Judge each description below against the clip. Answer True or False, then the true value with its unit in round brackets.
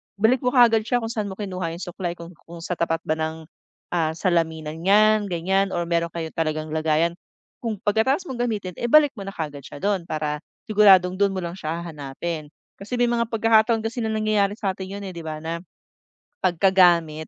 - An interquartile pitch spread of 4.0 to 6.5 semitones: True (4.7 semitones)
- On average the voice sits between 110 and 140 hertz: False (185 Hz)